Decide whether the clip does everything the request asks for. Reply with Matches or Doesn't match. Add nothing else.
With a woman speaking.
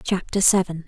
Matches